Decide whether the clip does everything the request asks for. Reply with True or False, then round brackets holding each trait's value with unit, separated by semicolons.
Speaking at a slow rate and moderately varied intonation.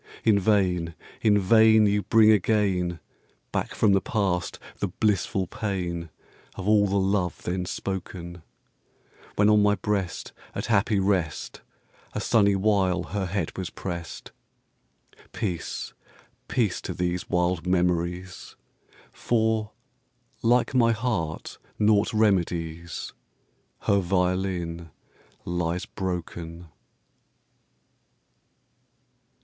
True (100 wpm; 3.0 semitones)